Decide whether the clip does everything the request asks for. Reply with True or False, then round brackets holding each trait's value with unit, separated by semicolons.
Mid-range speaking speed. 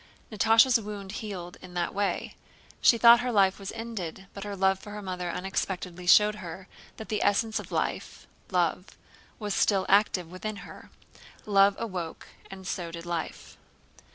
True (155 wpm)